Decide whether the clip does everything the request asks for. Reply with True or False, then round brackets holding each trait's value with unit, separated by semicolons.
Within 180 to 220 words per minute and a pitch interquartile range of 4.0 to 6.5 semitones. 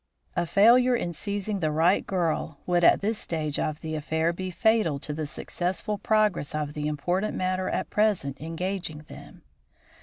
False (170 wpm; 4.6 semitones)